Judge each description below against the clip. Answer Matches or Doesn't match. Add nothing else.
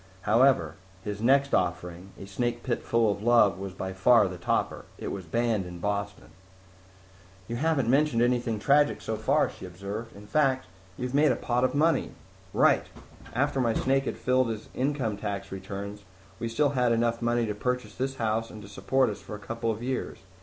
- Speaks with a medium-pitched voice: Doesn't match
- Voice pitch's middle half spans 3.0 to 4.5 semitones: Matches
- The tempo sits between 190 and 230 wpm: Matches